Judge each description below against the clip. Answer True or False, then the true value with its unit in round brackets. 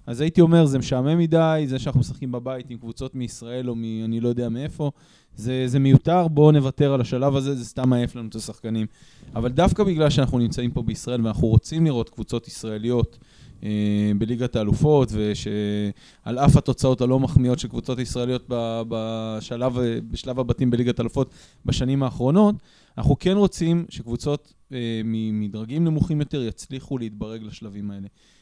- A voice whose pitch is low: True (125 Hz)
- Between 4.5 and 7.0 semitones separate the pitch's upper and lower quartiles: False (3.5 semitones)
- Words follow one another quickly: True (160 wpm)